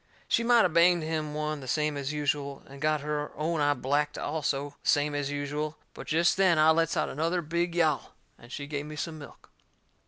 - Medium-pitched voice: Yes, medium, 150 Hz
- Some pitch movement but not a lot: No, narrow, 2.0 semitones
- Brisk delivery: Yes, fast, 215 wpm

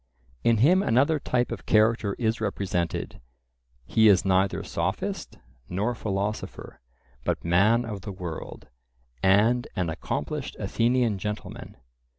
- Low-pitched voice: Yes, low, 105 Hz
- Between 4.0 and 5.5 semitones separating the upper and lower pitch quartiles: No, average, 3.5 semitones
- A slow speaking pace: Yes, slow, 120 wpm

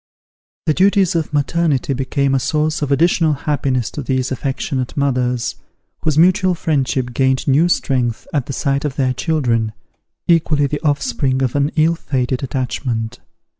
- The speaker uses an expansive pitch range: No, average, 3.2 semitones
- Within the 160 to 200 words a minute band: No, average, 150 wpm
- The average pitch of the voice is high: No, medium, 140 Hz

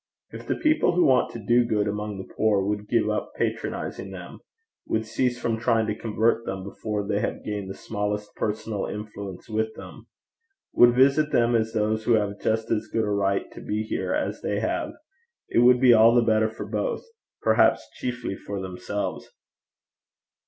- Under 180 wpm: No, average, 185 wpm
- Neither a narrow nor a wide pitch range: No, narrow, 2.2 semitones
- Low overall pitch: Yes, low, 110 Hz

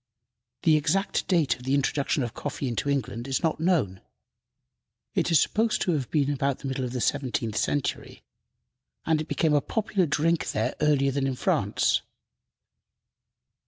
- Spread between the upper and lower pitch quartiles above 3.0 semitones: Yes, average, 3.5 semitones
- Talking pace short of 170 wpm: Yes, average, 160 wpm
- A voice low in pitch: No, medium, 145 Hz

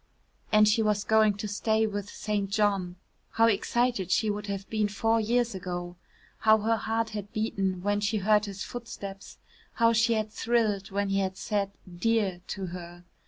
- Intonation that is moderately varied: No, narrow, 2.1 semitones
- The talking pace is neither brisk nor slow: Yes, average, 175 wpm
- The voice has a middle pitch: No, high, 210 Hz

